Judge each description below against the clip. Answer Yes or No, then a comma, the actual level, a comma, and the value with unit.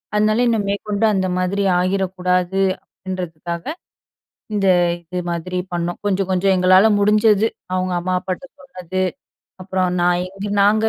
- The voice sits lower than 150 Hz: No, medium, 185 Hz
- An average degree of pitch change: No, narrow, 2.0 semitones